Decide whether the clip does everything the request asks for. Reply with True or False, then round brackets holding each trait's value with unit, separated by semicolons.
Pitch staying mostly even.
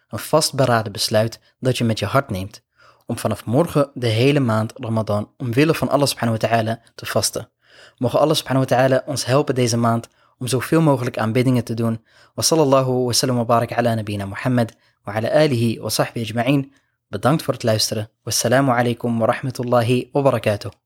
False (3.0 semitones)